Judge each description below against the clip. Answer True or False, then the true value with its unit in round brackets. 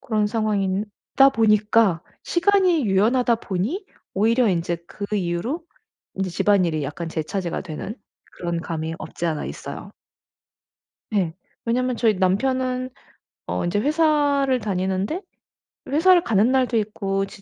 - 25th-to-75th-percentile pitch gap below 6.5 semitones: True (5.6 semitones)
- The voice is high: True (210 Hz)